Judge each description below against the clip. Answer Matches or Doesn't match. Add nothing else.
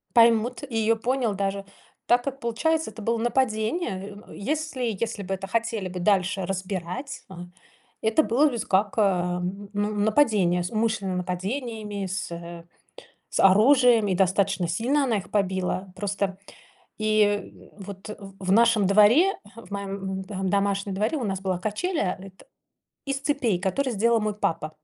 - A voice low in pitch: Doesn't match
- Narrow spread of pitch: Doesn't match